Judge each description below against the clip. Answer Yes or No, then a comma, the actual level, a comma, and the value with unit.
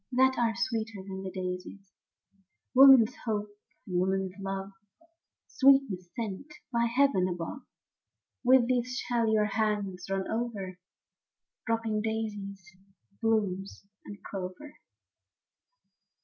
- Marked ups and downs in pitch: No, average, 3.6 semitones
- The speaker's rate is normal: No, slow, 105 wpm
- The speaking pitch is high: Yes, high, 215 Hz